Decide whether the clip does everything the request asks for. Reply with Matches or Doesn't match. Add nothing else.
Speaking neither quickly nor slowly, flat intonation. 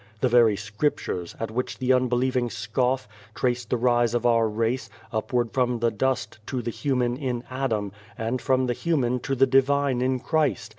Matches